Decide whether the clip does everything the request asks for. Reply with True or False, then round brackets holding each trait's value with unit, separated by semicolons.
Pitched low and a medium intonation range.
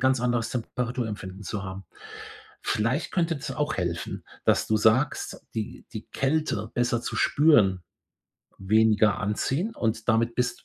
True (115 Hz; 3.9 semitones)